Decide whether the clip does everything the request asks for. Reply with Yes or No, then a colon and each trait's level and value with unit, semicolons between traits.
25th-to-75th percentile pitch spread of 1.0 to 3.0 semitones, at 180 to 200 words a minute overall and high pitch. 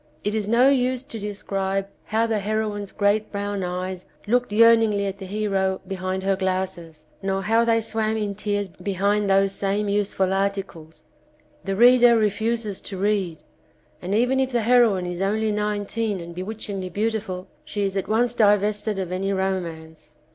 No: narrow, 2.4 semitones; average, 160 wpm; high, 205 Hz